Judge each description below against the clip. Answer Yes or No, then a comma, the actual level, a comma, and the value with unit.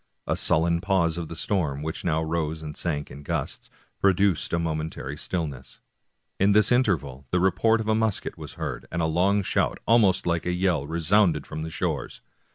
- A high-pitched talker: No, very low, 85 Hz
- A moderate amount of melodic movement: Yes, average, 3.8 semitones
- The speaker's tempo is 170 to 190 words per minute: Yes, average, 185 wpm